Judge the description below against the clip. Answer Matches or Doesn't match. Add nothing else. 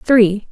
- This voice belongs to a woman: Matches